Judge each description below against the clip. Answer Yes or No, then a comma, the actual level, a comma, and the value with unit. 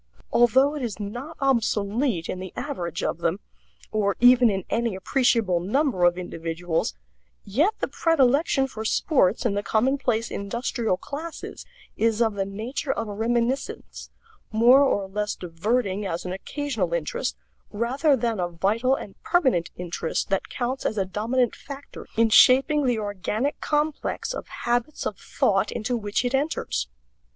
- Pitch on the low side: No, high, 225 Hz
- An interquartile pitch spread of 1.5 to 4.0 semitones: No, wide, 5.4 semitones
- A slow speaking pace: No, average, 150 wpm